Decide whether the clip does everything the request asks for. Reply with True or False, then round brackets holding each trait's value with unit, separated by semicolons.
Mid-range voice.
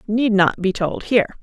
False (205 Hz)